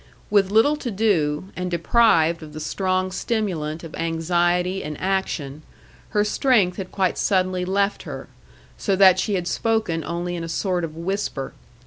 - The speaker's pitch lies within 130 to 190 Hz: Yes, medium, 185 Hz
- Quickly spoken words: No, average, 160 wpm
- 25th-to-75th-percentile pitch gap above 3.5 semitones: No, average, 3.2 semitones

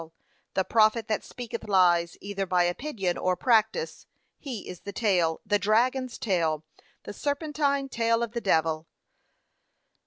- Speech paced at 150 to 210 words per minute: No, slow, 135 wpm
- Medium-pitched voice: No, high, 210 Hz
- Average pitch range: Yes, average, 4.9 semitones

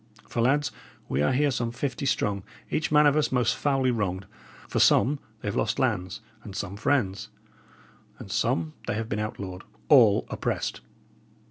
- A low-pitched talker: Yes, low, 115 Hz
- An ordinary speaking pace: Yes, average, 165 wpm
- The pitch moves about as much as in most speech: No, wide, 5.8 semitones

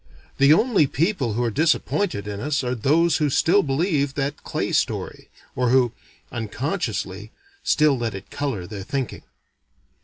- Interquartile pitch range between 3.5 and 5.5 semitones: Yes, average, 5.1 semitones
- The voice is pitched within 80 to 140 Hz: Yes, low, 135 Hz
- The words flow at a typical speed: Yes, average, 150 wpm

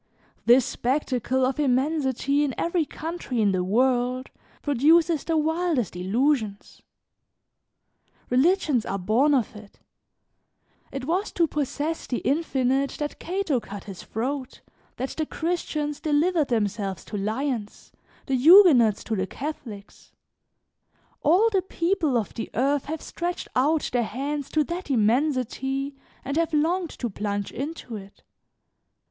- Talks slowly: Yes, slow, 130 wpm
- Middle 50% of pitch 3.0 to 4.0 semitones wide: No, average, 5.0 semitones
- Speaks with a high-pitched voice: Yes, very high, 275 Hz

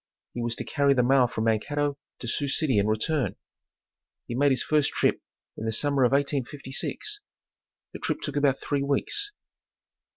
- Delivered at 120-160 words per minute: No, average, 170 wpm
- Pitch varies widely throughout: No, average, 3.2 semitones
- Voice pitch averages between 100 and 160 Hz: Yes, medium, 140 Hz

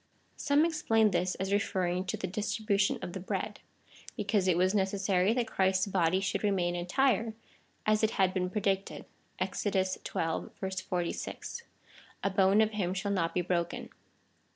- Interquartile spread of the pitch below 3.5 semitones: Yes, narrow, 2.5 semitones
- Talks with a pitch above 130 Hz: Yes, high, 190 Hz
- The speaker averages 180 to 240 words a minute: No, average, 155 wpm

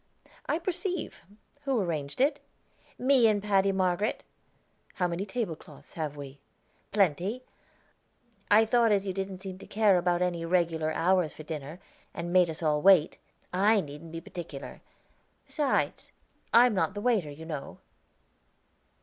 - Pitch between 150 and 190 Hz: Yes, medium, 185 Hz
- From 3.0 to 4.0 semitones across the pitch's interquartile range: No, average, 4.6 semitones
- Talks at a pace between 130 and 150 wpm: Yes, average, 145 wpm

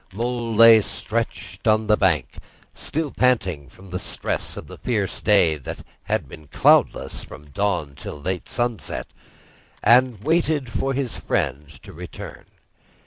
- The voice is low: Yes, low, 105 Hz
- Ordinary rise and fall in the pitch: No, wide, 6.1 semitones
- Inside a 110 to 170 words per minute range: Yes, average, 140 wpm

